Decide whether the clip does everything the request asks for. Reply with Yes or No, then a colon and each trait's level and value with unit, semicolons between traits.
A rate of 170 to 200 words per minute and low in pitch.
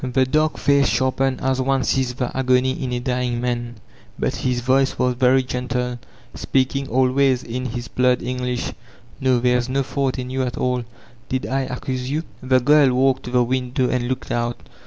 Yes: average, 195 wpm; low, 130 Hz